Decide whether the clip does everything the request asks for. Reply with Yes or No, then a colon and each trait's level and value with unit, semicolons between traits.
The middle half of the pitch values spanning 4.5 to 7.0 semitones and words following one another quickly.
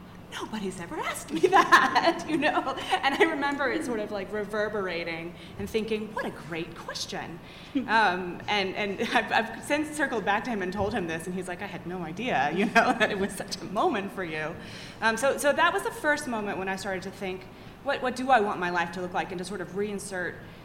Yes: wide, 5.4 semitones; fast, 230 wpm